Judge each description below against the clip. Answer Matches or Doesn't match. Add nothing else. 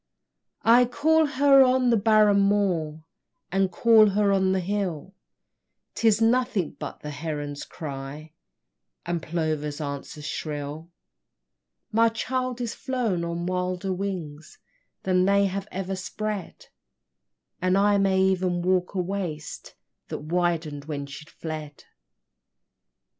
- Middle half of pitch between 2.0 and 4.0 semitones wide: Doesn't match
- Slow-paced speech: Matches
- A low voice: Doesn't match